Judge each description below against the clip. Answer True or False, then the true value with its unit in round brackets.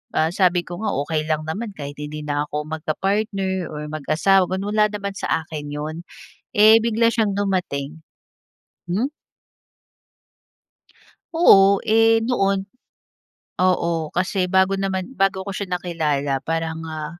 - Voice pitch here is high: False (180 Hz)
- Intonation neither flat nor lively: True (4.3 semitones)